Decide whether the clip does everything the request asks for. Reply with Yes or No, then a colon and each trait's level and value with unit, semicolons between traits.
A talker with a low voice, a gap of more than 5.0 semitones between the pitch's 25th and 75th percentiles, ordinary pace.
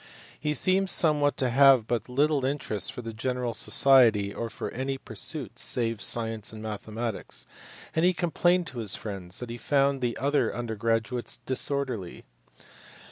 No: low, 125 Hz; average, 3.8 semitones; average, 155 wpm